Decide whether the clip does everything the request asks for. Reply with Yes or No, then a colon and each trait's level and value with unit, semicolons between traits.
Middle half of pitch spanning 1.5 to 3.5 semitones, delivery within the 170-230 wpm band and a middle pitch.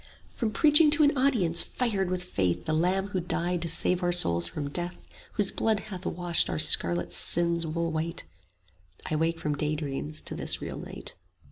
No: average, 3.9 semitones; average, 190 wpm; medium, 170 Hz